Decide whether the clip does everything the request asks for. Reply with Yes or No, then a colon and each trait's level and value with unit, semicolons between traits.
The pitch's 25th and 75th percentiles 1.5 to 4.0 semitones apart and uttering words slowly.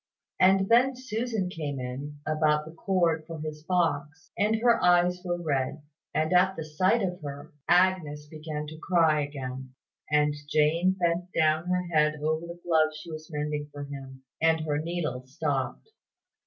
No: average, 3.1 semitones; average, 165 wpm